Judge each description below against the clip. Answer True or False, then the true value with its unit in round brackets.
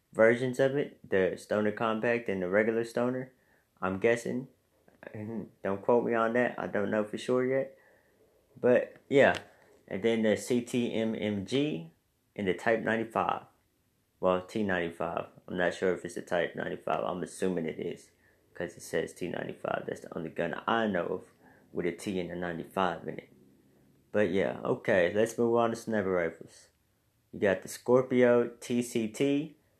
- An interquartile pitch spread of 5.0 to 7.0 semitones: False (4.3 semitones)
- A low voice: True (110 Hz)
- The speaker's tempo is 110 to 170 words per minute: True (160 wpm)